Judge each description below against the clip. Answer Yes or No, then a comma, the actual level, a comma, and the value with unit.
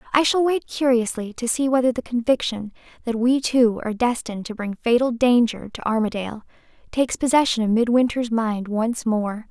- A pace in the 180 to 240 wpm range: No, average, 170 wpm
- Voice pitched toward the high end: Yes, high, 235 Hz